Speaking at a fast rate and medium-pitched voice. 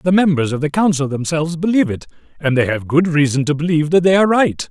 Yes: fast, 240 wpm; medium, 160 Hz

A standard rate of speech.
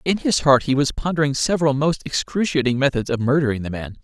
No: fast, 210 wpm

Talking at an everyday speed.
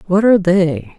Yes: average, 185 wpm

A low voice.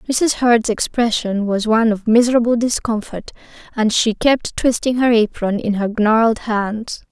No: high, 225 Hz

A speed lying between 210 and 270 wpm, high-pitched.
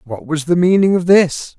No: fast, 230 wpm; medium, 170 Hz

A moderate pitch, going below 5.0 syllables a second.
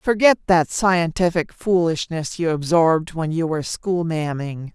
Yes: medium, 170 Hz; 4.6 syllables/s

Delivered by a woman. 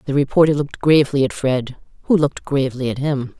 Yes: female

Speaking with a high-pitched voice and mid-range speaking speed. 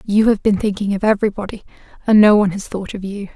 No: high, 205 Hz; fast, 230 wpm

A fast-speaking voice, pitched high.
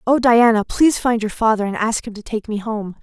Yes: fast, 260 wpm; high, 220 Hz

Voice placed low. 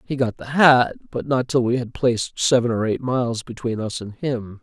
Yes: low, 120 Hz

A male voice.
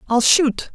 No: female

